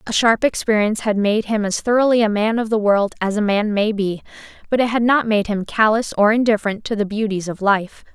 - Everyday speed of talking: No, fast, 235 wpm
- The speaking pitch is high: Yes, high, 215 Hz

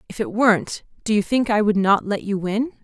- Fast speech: Yes, fast, 255 wpm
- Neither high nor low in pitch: No, high, 215 Hz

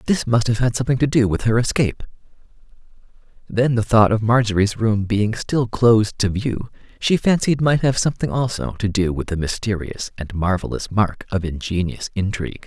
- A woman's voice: No, male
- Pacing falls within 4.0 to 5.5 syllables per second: Yes, 5.4 syllables/s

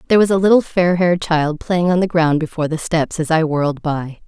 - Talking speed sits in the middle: No, fast, 255 wpm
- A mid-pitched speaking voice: Yes, medium, 165 Hz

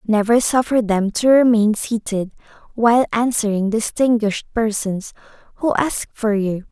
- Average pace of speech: No, slow, 125 wpm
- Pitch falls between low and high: No, high, 225 Hz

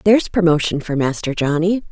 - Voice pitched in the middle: Yes, medium, 170 Hz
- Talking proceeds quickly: No, average, 155 wpm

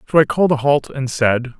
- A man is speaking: Yes, male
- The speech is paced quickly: Yes, fast, 265 wpm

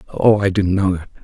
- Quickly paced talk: Yes, fast, 245 wpm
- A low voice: Yes, very low, 95 Hz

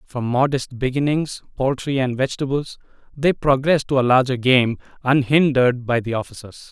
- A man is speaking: Yes, male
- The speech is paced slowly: Yes, slow, 115 wpm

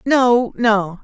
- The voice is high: Yes, high, 225 Hz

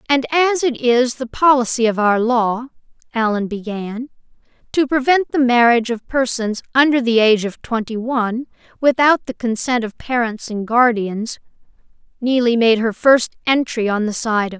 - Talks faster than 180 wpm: No, average, 160 wpm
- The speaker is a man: No, female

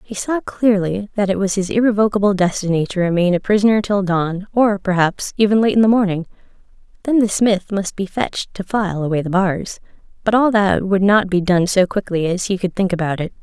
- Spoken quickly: Yes, fast, 215 wpm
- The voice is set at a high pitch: Yes, high, 195 Hz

